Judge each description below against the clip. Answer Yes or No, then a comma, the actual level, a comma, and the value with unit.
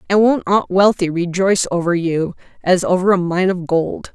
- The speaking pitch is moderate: Yes, medium, 180 Hz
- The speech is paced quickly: No, average, 190 wpm